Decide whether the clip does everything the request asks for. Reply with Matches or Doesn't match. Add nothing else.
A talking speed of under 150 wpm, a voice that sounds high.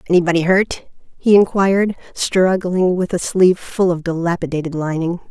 Doesn't match